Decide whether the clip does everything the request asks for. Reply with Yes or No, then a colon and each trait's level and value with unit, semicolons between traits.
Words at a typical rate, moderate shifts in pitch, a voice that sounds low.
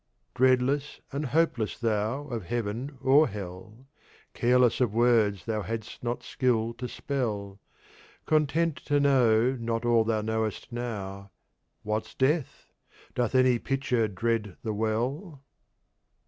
No: slow, 120 wpm; average, 3.4 semitones; low, 120 Hz